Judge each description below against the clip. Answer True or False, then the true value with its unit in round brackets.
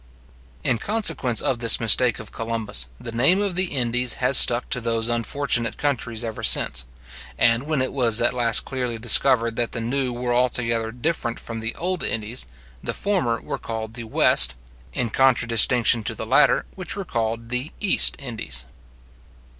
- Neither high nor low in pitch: False (120 Hz)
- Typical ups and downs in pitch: False (2.2 semitones)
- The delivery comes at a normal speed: True (170 wpm)